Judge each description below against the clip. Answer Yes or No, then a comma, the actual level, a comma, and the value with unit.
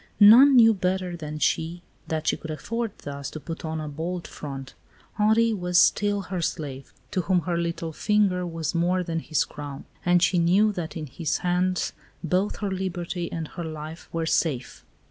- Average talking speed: Yes, average, 185 wpm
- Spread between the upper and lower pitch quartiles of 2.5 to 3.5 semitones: Yes, average, 2.8 semitones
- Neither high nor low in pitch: Yes, medium, 175 Hz